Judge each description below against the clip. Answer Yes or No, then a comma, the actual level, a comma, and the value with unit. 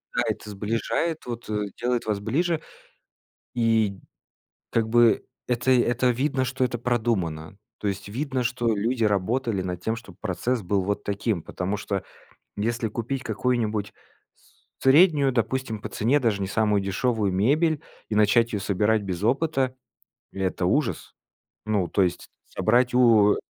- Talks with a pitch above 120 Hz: No, low, 115 Hz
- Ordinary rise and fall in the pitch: Yes, average, 3.6 semitones